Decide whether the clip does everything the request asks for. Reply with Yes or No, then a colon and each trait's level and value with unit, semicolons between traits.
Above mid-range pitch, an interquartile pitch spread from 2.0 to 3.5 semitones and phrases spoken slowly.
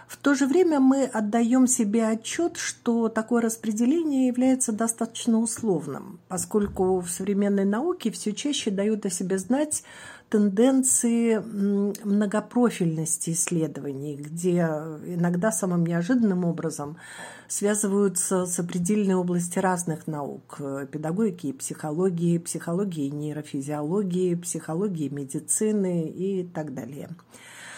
No: high, 195 Hz; average, 5.2 semitones; slow, 100 wpm